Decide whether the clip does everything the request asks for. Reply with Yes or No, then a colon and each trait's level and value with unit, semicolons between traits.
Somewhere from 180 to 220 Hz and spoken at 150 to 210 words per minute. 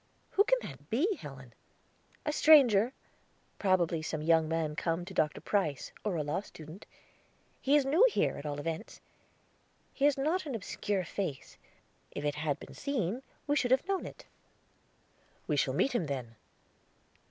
Yes: high, 190 Hz; average, 165 wpm